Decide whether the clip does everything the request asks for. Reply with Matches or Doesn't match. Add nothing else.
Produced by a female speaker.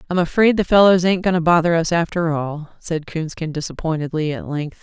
Matches